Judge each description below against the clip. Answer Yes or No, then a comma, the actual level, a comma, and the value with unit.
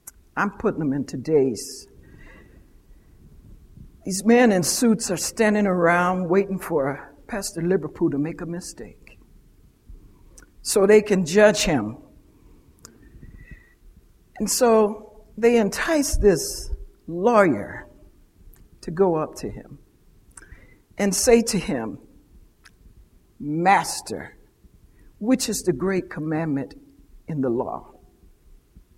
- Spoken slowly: Yes, slow, 100 wpm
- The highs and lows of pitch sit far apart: Yes, wide, 6.8 semitones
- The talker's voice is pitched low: No, medium, 185 Hz